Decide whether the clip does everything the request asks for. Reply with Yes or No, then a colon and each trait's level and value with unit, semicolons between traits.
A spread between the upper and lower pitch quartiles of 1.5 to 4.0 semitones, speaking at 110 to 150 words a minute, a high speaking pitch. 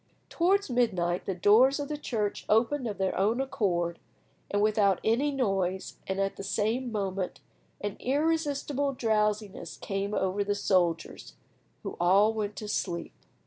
No: average, 4.4 semitones; average, 145 wpm; high, 210 Hz